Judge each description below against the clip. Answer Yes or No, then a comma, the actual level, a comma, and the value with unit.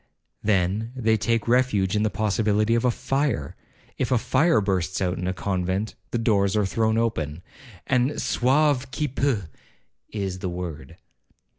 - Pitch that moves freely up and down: No, average, 4.8 semitones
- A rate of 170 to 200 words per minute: No, average, 155 wpm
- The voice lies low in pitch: Yes, low, 110 Hz